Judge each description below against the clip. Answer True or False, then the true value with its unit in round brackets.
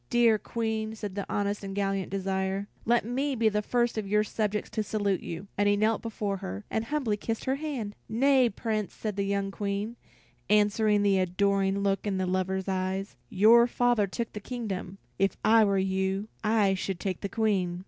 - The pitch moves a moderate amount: False (2.2 semitones)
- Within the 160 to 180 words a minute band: False (190 wpm)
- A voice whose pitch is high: True (205 Hz)